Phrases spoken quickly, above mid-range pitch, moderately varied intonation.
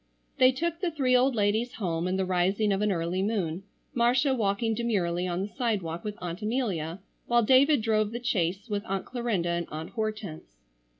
No: average, 185 wpm; high, 210 Hz; average, 5.0 semitones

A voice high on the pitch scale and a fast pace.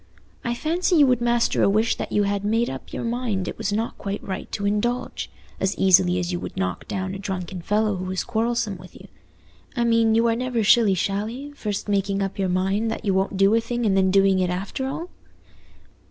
Yes: high, 205 Hz; fast, 225 wpm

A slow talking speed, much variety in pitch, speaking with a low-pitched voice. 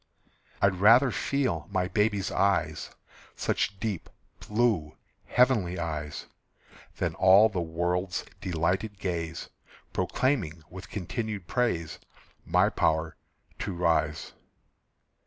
No: slow, 100 wpm; average, 4.3 semitones; very low, 95 Hz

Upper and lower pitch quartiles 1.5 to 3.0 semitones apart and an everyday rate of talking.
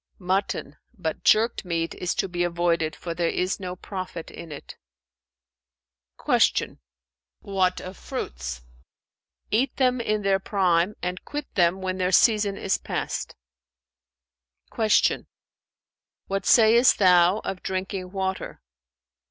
No: narrow, 2.4 semitones; slow, 120 wpm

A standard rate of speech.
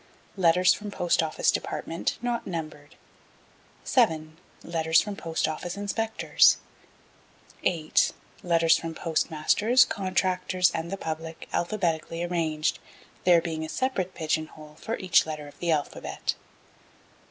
No: slow, 115 wpm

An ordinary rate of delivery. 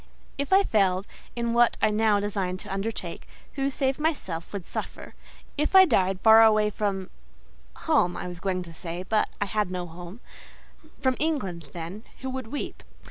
Yes: average, 165 wpm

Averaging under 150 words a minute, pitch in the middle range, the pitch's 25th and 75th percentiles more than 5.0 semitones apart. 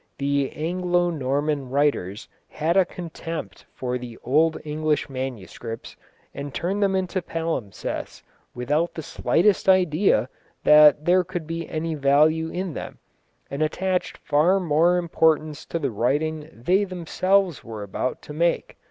No: slow, 135 wpm; medium, 155 Hz; average, 4.0 semitones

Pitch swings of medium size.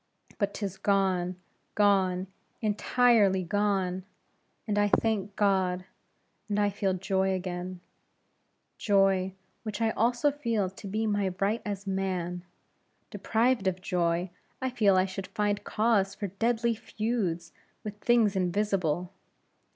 No: narrow, 2.3 semitones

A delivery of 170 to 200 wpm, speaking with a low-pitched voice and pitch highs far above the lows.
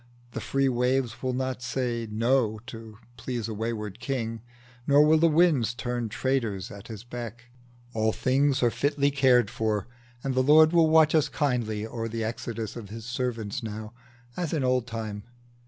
No: average, 175 wpm; low, 120 Hz; average, 3.2 semitones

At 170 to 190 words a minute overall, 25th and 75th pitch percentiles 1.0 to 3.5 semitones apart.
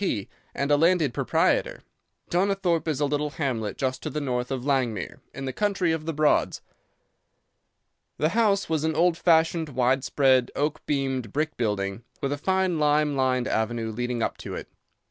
No: average, 175 wpm; average, 4.3 semitones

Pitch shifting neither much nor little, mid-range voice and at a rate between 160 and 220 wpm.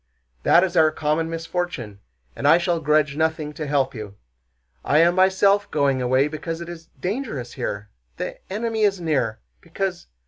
Yes: average, 3.9 semitones; medium, 160 Hz; average, 165 wpm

